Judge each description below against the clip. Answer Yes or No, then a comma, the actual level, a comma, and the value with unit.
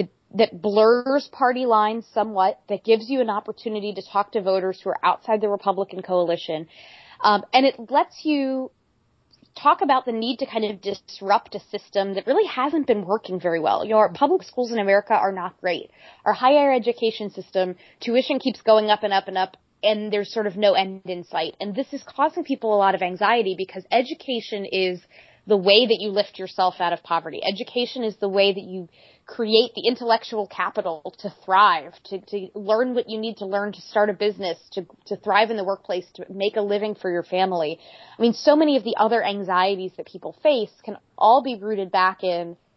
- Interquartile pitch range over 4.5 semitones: No, average, 3.6 semitones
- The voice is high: Yes, high, 210 Hz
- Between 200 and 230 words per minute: Yes, fast, 205 wpm